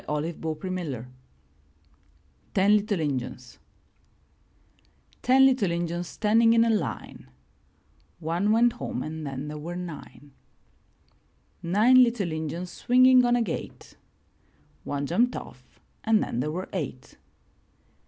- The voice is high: No, medium, 175 Hz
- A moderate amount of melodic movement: No, wide, 6.8 semitones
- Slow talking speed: Yes, slow, 130 wpm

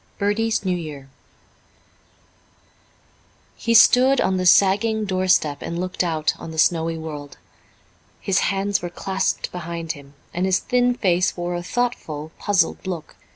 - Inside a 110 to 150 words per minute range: Yes, average, 140 wpm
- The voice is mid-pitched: Yes, medium, 180 Hz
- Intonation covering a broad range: No, average, 3.6 semitones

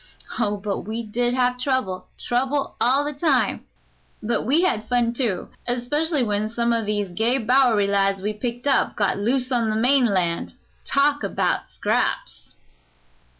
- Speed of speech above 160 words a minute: No, average, 150 wpm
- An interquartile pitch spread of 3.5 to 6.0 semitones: Yes, average, 3.8 semitones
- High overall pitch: Yes, high, 235 Hz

